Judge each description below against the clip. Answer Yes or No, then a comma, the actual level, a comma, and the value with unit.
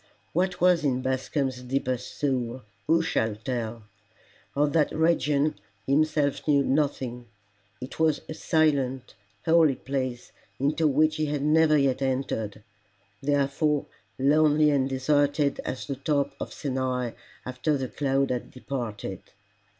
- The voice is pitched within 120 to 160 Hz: Yes, medium, 140 Hz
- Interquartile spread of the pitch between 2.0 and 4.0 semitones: Yes, average, 2.8 semitones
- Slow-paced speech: Yes, slow, 130 wpm